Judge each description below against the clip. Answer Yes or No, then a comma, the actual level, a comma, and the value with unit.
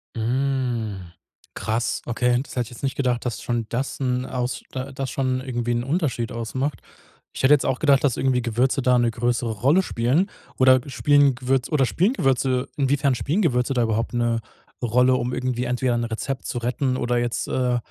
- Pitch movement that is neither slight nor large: No, narrow, 2.0 semitones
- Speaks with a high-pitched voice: No, low, 125 Hz